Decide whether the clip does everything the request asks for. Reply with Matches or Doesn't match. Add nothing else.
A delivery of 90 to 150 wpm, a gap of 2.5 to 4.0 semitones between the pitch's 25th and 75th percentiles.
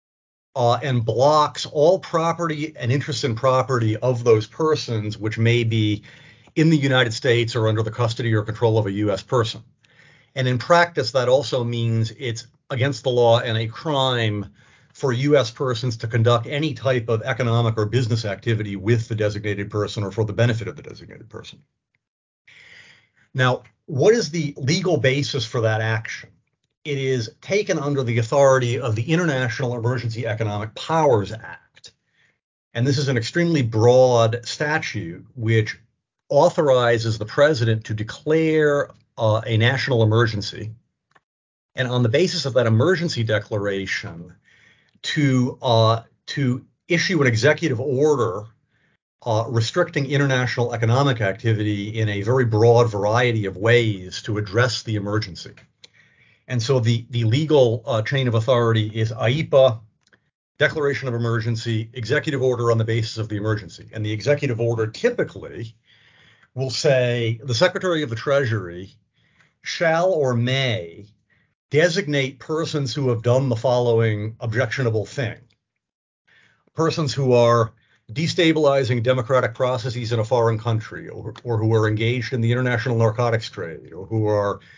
Matches